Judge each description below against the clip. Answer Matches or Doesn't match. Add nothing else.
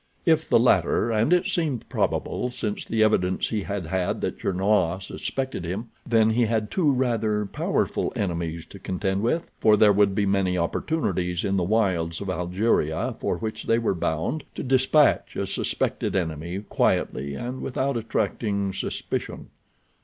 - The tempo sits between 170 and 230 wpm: Doesn't match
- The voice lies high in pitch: Doesn't match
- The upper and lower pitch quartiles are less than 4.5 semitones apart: Matches